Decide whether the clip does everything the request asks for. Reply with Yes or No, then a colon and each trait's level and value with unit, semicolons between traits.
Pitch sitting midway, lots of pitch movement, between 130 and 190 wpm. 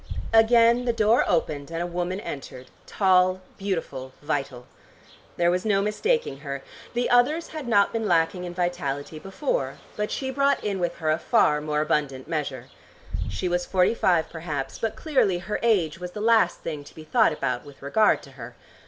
Yes: medium, 180 Hz; wide, 6.3 semitones; average, 180 wpm